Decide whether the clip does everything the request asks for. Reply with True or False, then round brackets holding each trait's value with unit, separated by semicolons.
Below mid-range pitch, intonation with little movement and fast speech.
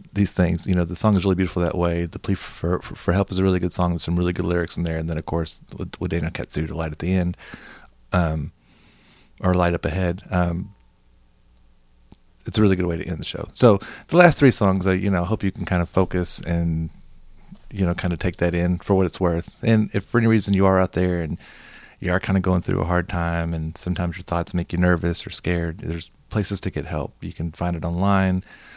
True (90 Hz; 1.9 semitones; 255 wpm)